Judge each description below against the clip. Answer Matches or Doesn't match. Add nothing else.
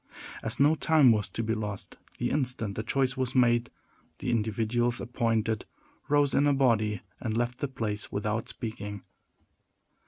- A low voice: Matches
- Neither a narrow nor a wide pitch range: Matches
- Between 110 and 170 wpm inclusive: Matches